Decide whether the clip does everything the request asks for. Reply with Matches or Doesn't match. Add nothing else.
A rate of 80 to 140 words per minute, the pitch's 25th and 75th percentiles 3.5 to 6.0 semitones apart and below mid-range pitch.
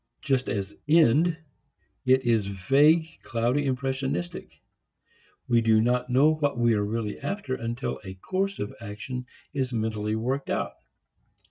Matches